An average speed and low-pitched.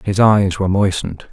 Yes: average, 180 wpm; very low, 95 Hz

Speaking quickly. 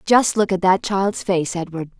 Yes: fast, 210 wpm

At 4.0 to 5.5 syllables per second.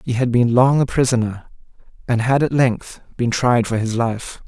Yes: 4.6 syllables/s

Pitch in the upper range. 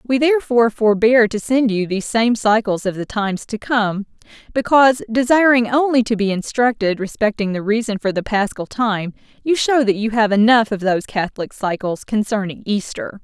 Yes: high, 220 Hz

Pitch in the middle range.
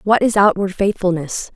No: high, 195 Hz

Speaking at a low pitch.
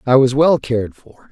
Yes: low, 130 Hz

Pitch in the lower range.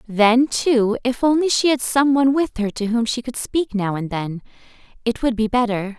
No: high, 240 Hz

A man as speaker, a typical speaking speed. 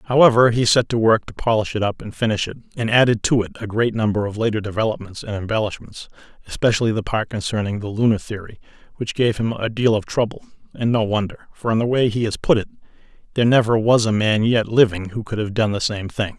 No: male; fast, 225 wpm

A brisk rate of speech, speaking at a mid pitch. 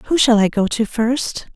No: fast, 230 wpm; high, 230 Hz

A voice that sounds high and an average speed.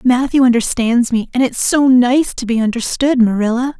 Yes: high, 245 Hz; average, 175 wpm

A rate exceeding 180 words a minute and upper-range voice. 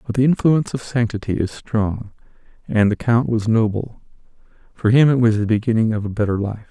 No: average, 195 wpm; low, 110 Hz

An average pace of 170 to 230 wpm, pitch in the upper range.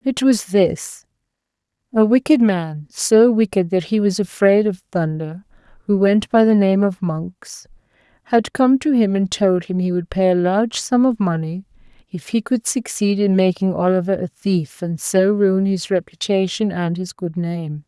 Yes: average, 175 wpm; high, 195 Hz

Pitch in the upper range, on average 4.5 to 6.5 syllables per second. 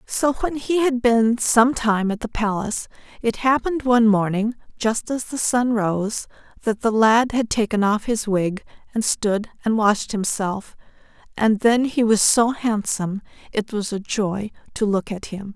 No: high, 220 Hz; 4.3 syllables/s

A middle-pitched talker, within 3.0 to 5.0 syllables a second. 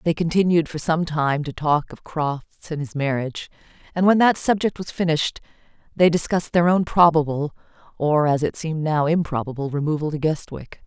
No: medium, 155 Hz; 5.4 syllables/s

